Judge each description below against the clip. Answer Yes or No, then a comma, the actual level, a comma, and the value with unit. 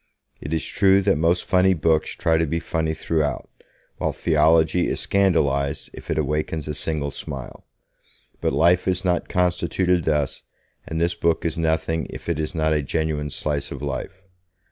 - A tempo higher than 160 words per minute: Yes, average, 170 wpm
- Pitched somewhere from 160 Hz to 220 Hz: No, very low, 80 Hz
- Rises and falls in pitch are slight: Yes, narrow, 2.3 semitones